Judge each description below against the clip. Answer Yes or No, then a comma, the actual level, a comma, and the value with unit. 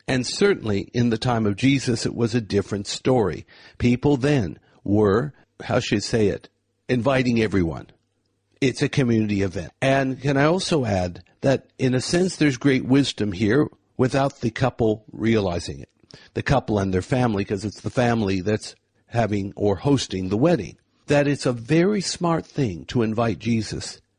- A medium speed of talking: Yes, average, 170 wpm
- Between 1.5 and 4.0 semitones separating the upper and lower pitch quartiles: No, average, 4.9 semitones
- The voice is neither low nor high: No, low, 120 Hz